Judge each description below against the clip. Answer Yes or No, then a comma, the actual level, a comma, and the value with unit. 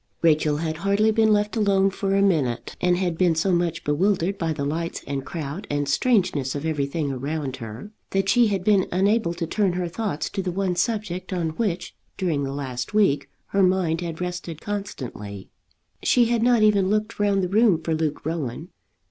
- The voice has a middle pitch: Yes, medium, 175 Hz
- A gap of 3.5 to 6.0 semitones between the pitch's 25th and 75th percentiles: Yes, average, 4.6 semitones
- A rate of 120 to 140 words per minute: No, average, 190 wpm